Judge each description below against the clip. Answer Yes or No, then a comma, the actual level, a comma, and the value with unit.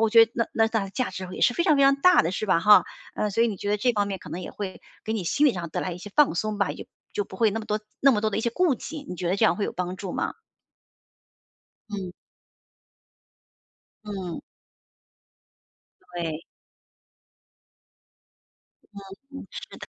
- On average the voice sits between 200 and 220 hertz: Yes, high, 210 Hz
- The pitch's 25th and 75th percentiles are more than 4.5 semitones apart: No, average, 3.6 semitones